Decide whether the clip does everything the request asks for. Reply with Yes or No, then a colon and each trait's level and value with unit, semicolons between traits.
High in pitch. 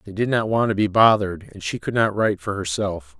No: low, 105 Hz